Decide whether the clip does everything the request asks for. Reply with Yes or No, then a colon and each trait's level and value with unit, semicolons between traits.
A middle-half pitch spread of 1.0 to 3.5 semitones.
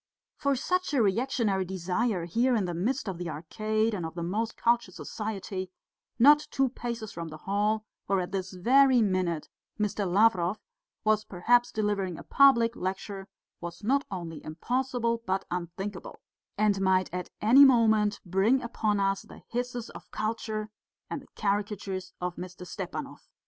No: average, 4.0 semitones